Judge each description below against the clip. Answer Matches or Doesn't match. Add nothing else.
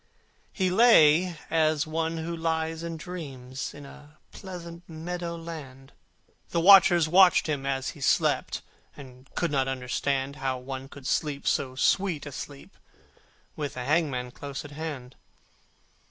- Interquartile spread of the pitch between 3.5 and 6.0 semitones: Matches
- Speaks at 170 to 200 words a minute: Doesn't match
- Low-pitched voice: Doesn't match